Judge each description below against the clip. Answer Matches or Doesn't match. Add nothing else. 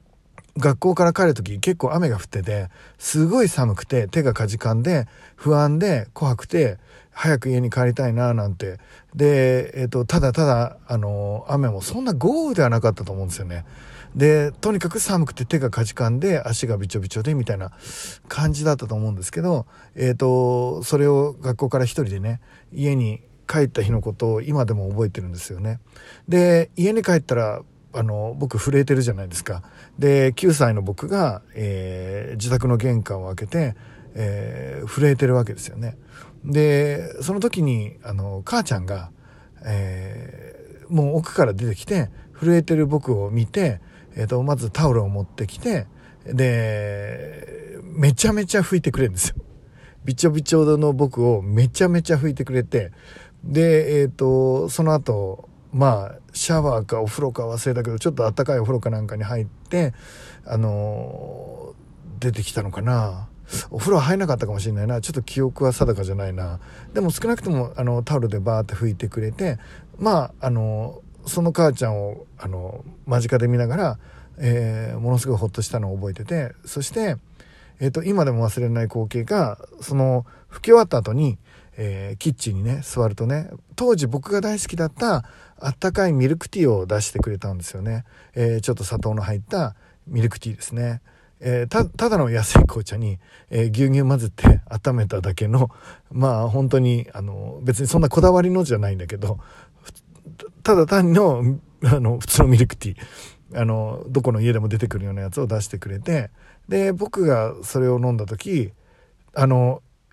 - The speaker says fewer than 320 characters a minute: Doesn't match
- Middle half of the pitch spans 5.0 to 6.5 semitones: Matches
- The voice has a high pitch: Doesn't match